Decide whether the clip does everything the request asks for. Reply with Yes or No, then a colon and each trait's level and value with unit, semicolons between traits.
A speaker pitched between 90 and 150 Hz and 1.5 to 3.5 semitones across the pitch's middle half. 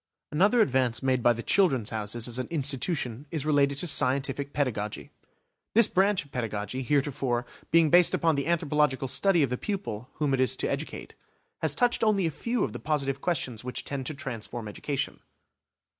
No: medium, 140 Hz; average, 4.5 semitones